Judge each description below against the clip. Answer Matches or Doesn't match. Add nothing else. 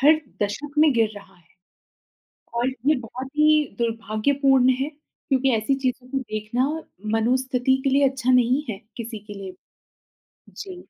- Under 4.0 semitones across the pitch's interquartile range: Matches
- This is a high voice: Matches